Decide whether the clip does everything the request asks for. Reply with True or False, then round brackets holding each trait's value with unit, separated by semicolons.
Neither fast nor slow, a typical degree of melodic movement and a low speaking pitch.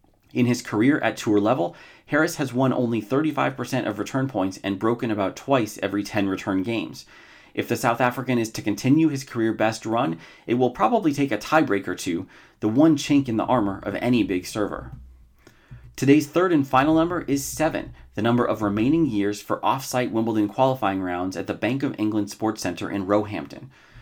True (190 wpm; 4.6 semitones; 115 Hz)